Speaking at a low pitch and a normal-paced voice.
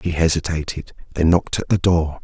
Yes: very low, 85 Hz; average, 190 wpm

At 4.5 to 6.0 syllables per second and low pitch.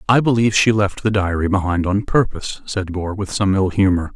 Yes: 5.6 syllables/s; low, 100 Hz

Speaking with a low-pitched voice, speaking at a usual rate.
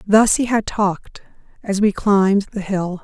No: high, 200 Hz; average, 180 wpm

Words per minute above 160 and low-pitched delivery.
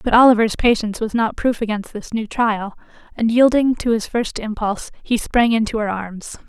No: average, 195 wpm; high, 220 Hz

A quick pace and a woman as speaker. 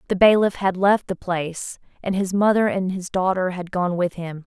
Yes: fast, 210 wpm; female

